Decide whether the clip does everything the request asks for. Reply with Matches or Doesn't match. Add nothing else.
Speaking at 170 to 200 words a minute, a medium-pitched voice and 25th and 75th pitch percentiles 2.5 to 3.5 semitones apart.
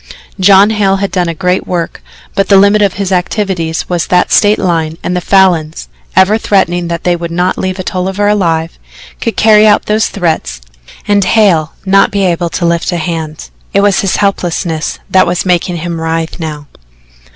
Matches